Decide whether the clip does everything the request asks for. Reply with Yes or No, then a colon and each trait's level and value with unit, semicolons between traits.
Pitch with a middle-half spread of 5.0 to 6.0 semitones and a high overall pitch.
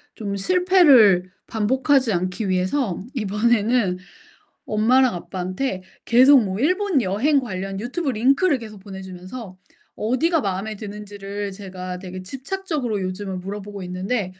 Yes: wide, 5.4 semitones; high, 210 Hz